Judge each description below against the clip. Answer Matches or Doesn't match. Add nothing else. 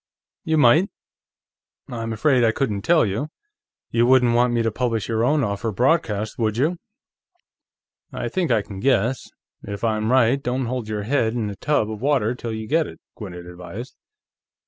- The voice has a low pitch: Matches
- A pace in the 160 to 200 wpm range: Matches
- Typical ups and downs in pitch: Matches